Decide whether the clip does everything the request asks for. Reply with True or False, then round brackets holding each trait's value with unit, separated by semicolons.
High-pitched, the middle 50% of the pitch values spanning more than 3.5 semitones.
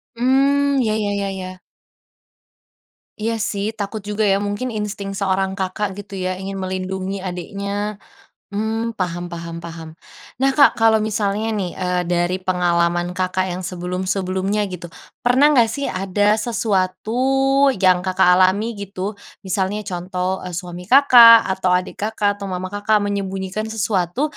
False (195 Hz; 2.8 semitones)